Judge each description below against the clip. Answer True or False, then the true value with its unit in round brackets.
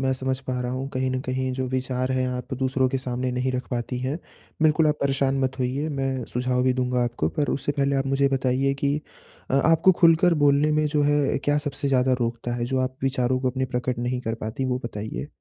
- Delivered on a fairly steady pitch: True (1.6 semitones)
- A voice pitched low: True (130 Hz)